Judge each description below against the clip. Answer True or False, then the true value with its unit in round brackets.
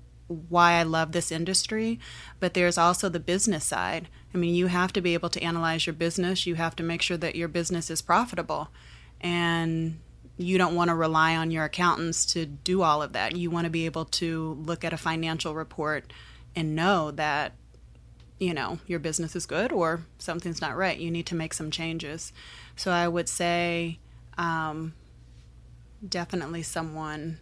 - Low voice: False (165 Hz)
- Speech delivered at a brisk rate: False (180 wpm)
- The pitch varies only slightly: True (1.4 semitones)